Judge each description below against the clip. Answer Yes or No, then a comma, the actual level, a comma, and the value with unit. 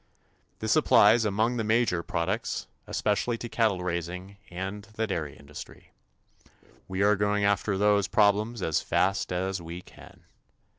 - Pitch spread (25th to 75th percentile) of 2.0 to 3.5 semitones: Yes, average, 3.0 semitones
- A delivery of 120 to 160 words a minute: Yes, average, 140 wpm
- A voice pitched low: Yes, low, 100 Hz